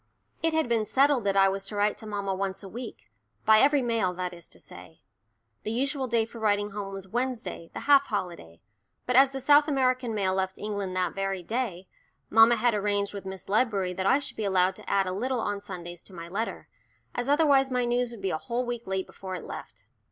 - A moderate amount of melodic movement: Yes, average, 4.5 semitones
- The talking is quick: Yes, fast, 225 wpm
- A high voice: Yes, high, 210 Hz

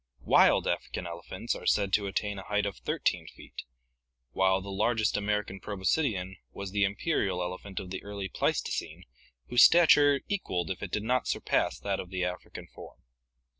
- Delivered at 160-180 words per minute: Yes, average, 170 wpm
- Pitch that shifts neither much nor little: No, narrow, 2.1 semitones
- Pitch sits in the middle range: No, low, 100 Hz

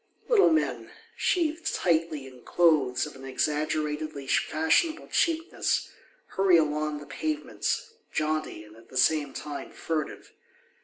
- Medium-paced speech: No, slow, 120 wpm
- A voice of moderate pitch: Yes, medium, 155 Hz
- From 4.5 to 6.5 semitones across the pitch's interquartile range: Yes, average, 4.8 semitones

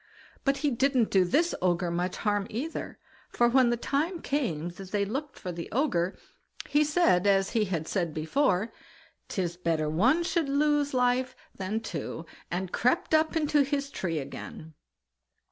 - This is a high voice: Yes, high, 225 Hz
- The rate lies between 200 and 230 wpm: No, average, 160 wpm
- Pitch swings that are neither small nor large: No, wide, 8.0 semitones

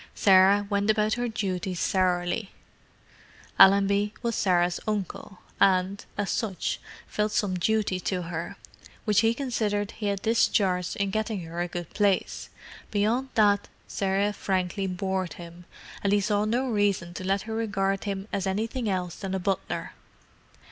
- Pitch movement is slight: Yes, narrow, 2.3 semitones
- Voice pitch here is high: Yes, high, 200 Hz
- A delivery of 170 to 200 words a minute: No, average, 150 wpm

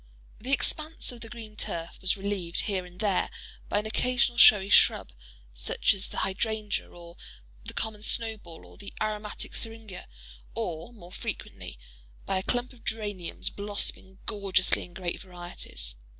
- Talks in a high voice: Yes, high, 205 Hz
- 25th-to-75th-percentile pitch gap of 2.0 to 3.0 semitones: No, average, 3.4 semitones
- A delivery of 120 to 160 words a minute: Yes, average, 150 wpm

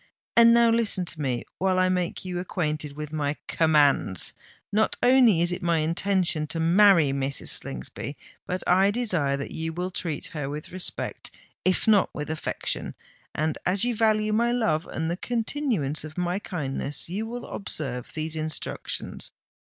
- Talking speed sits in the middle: Yes, average, 160 wpm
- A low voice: No, medium, 175 Hz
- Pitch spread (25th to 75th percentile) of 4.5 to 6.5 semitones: Yes, average, 5.0 semitones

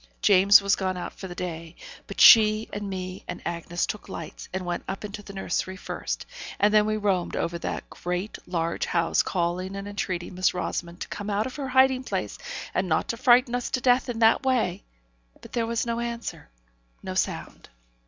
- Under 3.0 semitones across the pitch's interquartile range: No, average, 4.0 semitones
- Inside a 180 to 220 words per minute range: Yes, average, 195 wpm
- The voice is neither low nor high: No, high, 200 Hz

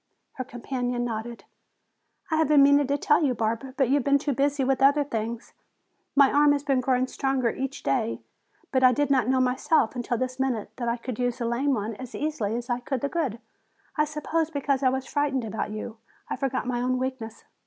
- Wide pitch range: No, average, 2.8 semitones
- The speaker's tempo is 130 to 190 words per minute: No, fast, 205 wpm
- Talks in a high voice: Yes, very high, 260 Hz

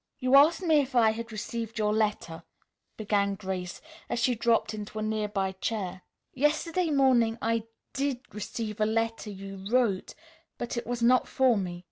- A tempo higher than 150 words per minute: Yes, average, 165 wpm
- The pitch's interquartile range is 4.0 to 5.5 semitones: No, average, 3.3 semitones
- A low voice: No, high, 225 Hz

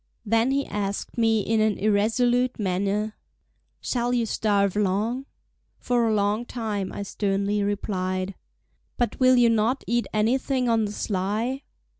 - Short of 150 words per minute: Yes, average, 140 wpm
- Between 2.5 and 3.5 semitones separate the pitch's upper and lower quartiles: Yes, average, 3.0 semitones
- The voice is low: No, high, 215 Hz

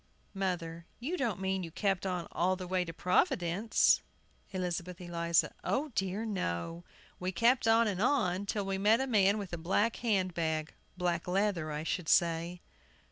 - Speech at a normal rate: Yes, average, 170 wpm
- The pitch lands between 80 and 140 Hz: No, medium, 185 Hz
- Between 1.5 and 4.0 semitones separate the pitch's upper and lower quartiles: Yes, average, 3.2 semitones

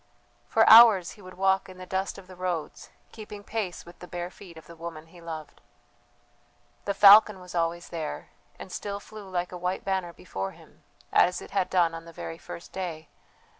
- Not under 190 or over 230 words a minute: Yes, average, 200 wpm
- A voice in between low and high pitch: Yes, medium, 180 Hz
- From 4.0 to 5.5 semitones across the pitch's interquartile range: No, narrow, 2.4 semitones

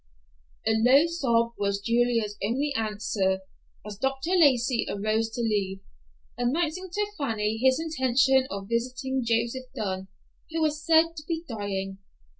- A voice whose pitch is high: Yes, high, 240 Hz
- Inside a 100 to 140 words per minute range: Yes, slow, 135 wpm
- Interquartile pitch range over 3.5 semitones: Yes, average, 4.9 semitones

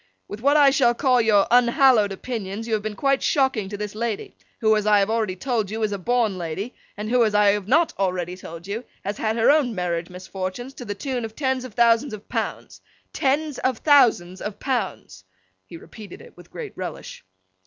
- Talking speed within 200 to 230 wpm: Yes, fast, 205 wpm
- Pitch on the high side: Yes, high, 220 Hz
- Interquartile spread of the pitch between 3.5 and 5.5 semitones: Yes, average, 4.1 semitones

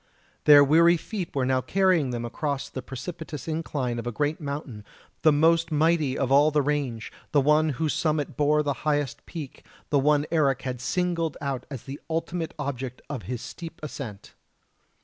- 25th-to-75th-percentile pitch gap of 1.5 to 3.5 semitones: Yes, average, 3.2 semitones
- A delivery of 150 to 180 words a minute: Yes, average, 175 wpm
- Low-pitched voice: No, medium, 145 Hz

